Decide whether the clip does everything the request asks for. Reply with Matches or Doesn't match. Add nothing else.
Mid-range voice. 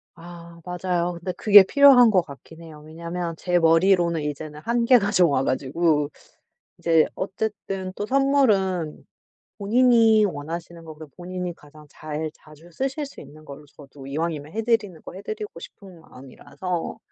Matches